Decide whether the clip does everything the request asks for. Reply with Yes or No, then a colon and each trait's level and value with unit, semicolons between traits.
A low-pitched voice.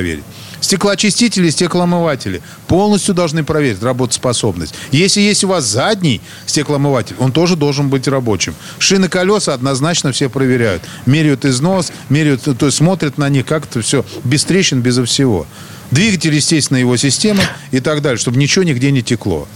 No: medium, 145 Hz